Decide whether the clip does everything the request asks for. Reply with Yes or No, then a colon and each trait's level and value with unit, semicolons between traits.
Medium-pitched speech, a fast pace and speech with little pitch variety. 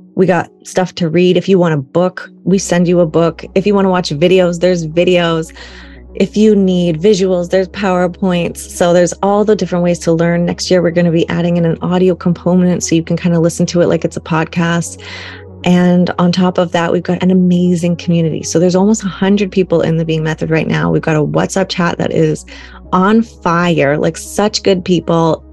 Yes: medium, 175 Hz; fast, 220 wpm; narrow, 1.6 semitones